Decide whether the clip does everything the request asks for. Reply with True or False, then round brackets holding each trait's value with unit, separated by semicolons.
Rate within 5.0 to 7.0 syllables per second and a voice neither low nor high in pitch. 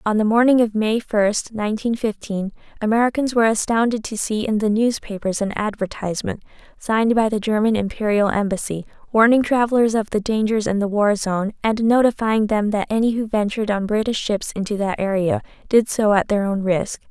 False (5.5 syllables/s; 215 Hz)